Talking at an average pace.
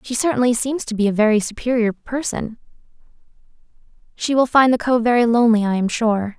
Yes: average, 180 wpm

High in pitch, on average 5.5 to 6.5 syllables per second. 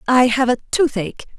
Yes: very high, 250 Hz; 5.9 syllables/s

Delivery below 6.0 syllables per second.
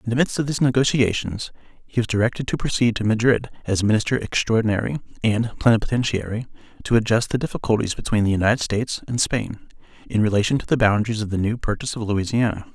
No: 6.7 syllables/s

